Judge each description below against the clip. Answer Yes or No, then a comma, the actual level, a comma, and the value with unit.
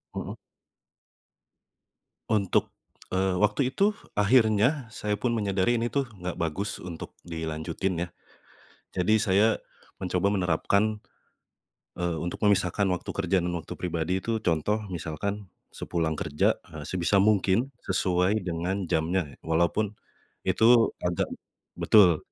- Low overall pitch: Yes, very low, 95 Hz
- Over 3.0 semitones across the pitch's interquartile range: Yes, average, 3.4 semitones